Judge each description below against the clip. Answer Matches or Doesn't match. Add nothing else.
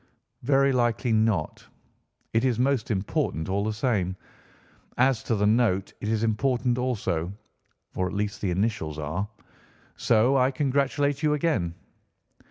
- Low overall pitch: Matches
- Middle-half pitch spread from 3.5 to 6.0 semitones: Matches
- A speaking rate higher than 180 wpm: Doesn't match